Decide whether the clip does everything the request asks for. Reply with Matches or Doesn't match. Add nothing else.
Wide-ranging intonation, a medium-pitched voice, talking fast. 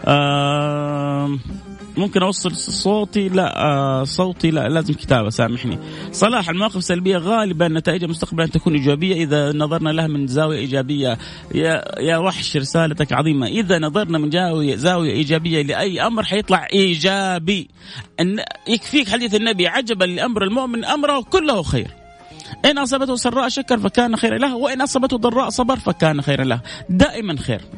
Matches